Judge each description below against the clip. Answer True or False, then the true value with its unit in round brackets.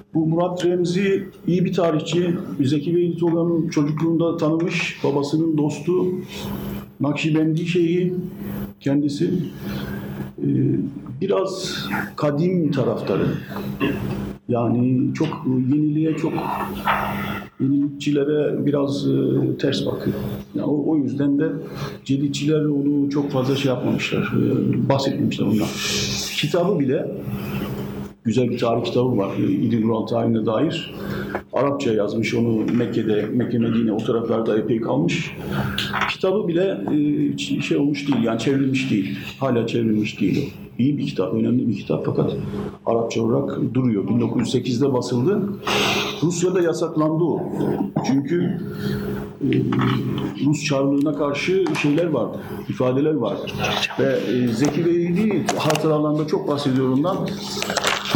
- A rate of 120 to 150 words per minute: False (105 wpm)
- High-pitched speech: False (145 Hz)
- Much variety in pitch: True (6.0 semitones)